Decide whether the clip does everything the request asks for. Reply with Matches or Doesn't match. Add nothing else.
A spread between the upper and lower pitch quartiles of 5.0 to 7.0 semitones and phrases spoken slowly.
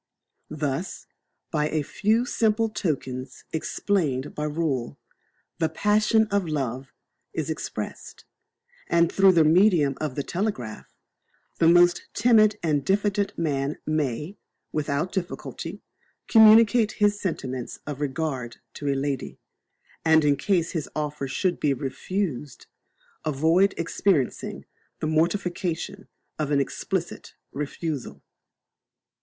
Matches